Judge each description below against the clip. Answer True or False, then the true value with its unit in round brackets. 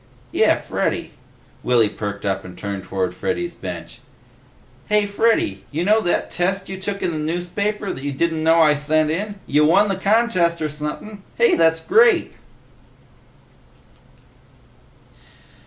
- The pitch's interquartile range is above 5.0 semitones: True (5.5 semitones)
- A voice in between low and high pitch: True (170 Hz)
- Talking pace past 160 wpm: False (145 wpm)